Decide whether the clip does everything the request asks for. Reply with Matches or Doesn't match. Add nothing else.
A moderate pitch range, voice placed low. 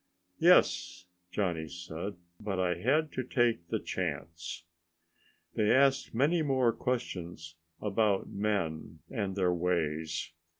Doesn't match